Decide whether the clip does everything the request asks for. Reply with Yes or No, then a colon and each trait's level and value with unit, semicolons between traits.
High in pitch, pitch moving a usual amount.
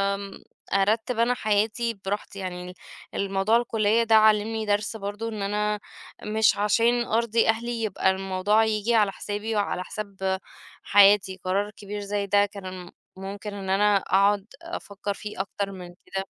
No: high, 205 Hz; narrow, 1.9 semitones